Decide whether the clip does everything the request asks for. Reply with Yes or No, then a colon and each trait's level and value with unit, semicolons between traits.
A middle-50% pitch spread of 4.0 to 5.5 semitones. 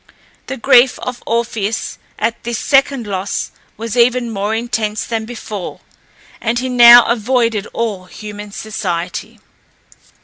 No: narrow, 2.5 semitones